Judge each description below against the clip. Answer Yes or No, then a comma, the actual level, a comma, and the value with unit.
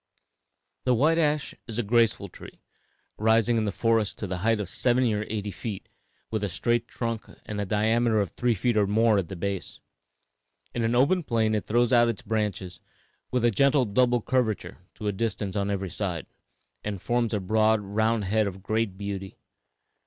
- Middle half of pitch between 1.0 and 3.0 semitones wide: Yes, average, 2.7 semitones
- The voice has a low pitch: Yes, low, 110 Hz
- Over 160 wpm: Yes, average, 190 wpm